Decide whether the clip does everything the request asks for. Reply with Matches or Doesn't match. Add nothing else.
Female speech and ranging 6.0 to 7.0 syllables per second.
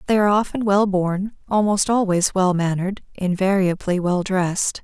Doesn't match